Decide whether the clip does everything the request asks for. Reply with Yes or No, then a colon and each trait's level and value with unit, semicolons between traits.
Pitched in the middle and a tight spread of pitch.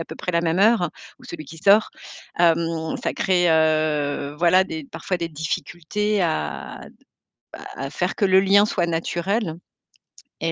No: medium, 170 Hz; average, 3.1 semitones